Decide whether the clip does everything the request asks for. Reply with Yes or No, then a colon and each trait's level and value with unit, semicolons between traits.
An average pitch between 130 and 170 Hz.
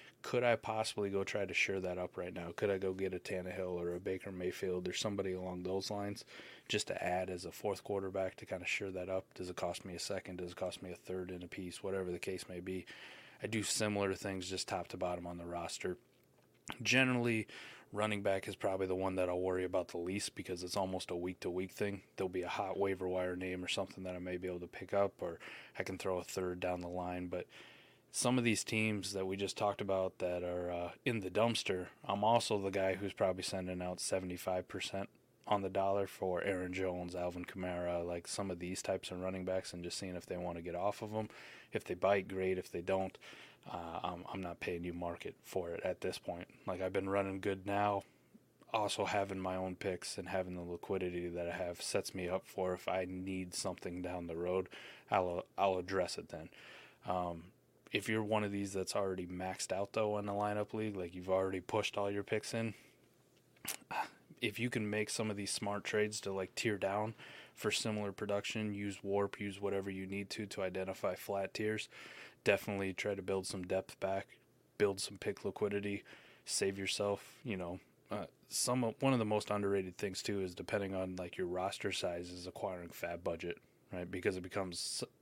No: very low, 95 Hz